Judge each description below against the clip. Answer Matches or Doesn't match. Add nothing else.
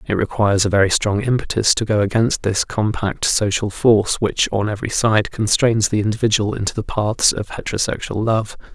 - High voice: Doesn't match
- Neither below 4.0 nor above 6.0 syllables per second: Matches